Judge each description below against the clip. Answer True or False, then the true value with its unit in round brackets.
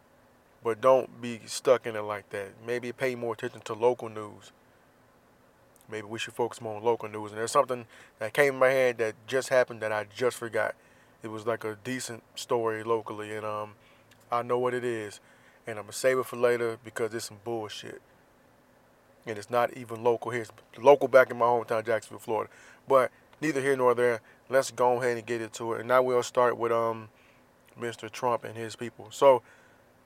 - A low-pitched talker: True (115 Hz)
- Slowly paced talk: False (200 wpm)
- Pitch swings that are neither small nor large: False (2.1 semitones)